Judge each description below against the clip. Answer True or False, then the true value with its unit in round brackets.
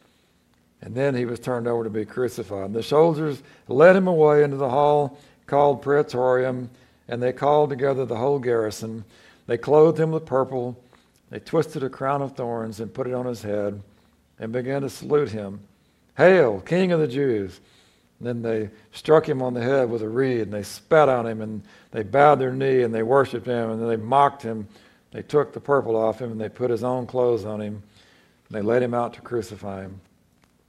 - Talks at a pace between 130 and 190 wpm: False (205 wpm)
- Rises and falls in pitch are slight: False (4.1 semitones)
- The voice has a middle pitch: False (120 Hz)